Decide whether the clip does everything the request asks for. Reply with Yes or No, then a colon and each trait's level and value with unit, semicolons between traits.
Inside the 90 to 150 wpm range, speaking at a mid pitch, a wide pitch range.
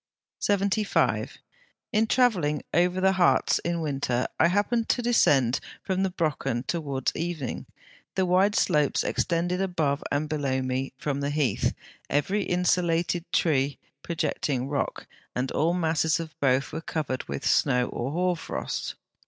No: average, 140 wpm; medium, 160 Hz; average, 4.4 semitones